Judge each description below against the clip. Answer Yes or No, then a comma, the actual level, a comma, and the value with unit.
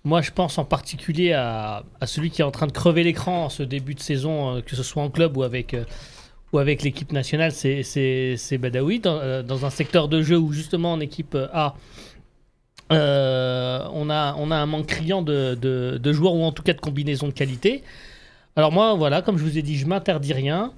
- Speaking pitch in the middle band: Yes, medium, 150 Hz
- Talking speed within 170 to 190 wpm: No, fast, 220 wpm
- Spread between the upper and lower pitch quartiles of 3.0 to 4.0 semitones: Yes, average, 3.3 semitones